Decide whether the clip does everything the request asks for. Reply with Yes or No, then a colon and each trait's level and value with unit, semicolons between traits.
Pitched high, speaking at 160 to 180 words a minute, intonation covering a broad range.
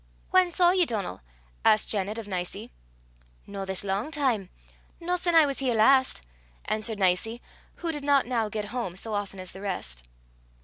Yes: high, 220 Hz; average, 175 wpm; wide, 6.3 semitones